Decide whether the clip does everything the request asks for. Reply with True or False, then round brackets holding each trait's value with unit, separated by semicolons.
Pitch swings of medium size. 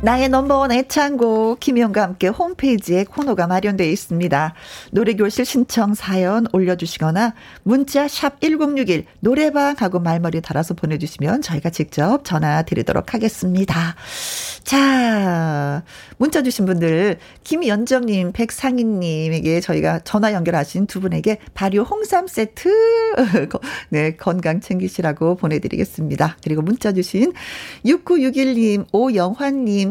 False (6.9 semitones)